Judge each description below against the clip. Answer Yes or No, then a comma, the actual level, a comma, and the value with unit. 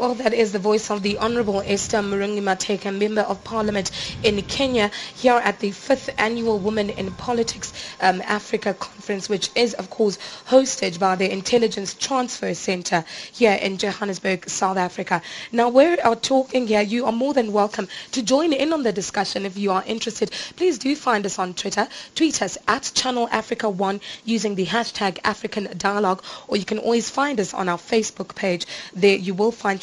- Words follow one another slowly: No, average, 190 wpm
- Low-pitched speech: No, high, 210 Hz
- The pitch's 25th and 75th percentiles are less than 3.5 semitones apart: Yes, average, 3.0 semitones